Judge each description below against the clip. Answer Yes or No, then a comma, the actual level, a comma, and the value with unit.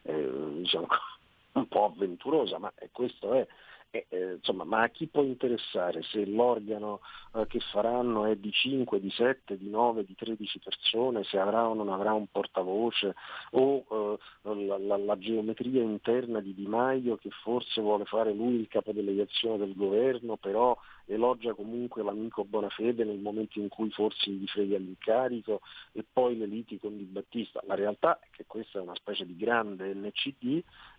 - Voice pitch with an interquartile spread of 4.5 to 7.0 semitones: No, average, 2.7 semitones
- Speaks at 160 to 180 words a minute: Yes, fast, 170 wpm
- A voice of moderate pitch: No, low, 110 Hz